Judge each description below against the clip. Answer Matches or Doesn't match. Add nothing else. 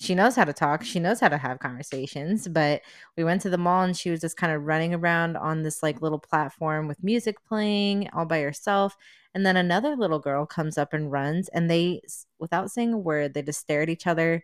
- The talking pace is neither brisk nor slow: Doesn't match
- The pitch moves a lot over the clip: Doesn't match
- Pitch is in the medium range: Matches